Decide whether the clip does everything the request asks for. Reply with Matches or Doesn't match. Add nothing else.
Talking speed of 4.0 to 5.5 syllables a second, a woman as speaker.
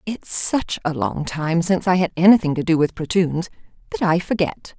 Matches